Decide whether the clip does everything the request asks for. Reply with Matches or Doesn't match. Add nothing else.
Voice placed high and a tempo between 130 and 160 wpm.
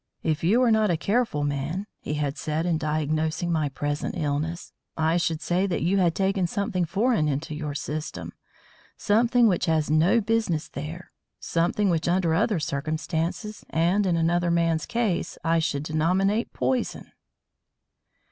Doesn't match